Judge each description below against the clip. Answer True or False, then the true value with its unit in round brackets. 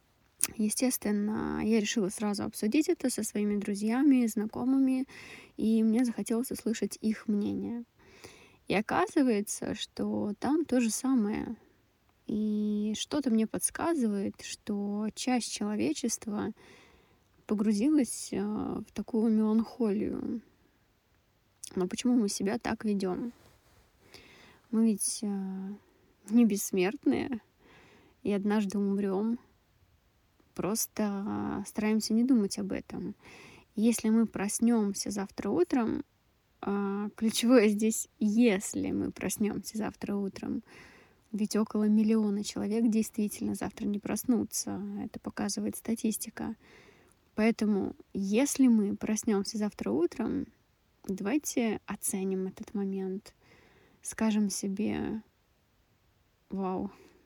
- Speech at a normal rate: False (95 wpm)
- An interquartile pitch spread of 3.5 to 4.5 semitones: False (2.6 semitones)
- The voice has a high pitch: True (215 Hz)